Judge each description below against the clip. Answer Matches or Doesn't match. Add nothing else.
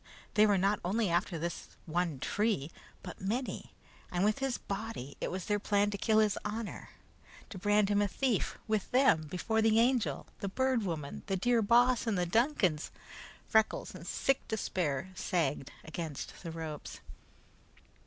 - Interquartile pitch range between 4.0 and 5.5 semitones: Matches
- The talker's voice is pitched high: Matches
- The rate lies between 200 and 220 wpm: Doesn't match